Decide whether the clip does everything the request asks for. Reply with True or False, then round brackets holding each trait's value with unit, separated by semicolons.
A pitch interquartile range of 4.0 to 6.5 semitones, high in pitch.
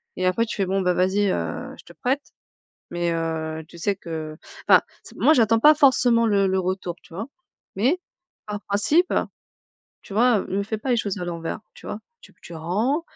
True (4.8 semitones; 200 Hz)